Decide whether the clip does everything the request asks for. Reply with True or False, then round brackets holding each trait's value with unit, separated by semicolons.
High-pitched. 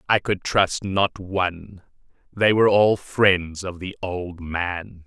False (95 Hz)